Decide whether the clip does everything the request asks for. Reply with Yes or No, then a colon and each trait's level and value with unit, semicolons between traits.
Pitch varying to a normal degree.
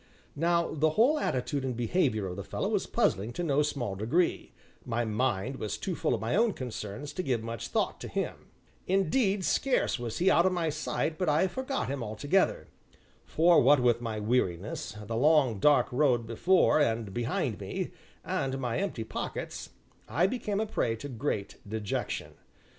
No: wide, 7.1 semitones